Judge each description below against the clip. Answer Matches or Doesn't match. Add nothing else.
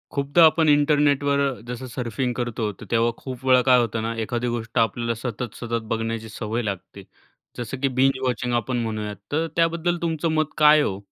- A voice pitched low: Matches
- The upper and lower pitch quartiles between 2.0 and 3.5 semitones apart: Doesn't match